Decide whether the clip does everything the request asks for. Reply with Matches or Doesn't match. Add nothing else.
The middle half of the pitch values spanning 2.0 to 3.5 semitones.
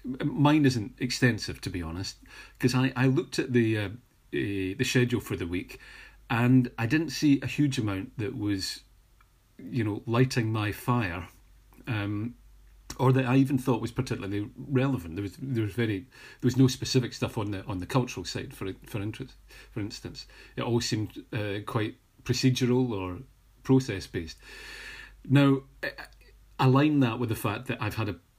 Doesn't match